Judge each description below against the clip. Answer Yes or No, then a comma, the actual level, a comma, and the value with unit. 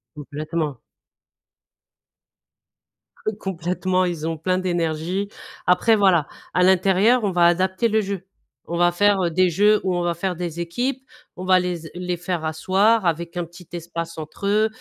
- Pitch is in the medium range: Yes, medium, 180 Hz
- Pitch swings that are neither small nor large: No, narrow, 2.2 semitones